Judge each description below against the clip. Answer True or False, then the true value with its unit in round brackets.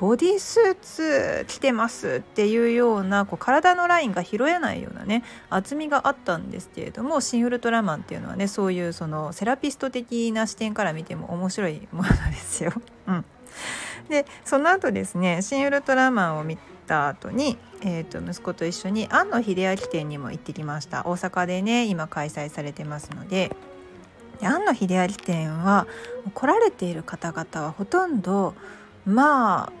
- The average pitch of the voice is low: False (200 Hz)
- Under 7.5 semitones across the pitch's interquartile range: True (6.5 semitones)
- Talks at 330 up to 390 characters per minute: True (345 characters per minute)